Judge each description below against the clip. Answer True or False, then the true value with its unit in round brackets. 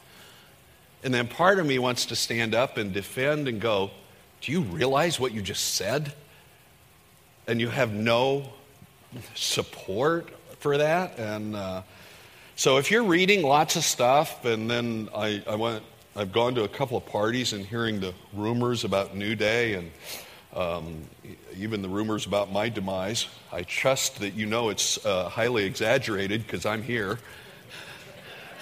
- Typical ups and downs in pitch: True (4.5 semitones)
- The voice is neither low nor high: False (115 Hz)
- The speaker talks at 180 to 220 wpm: False (155 wpm)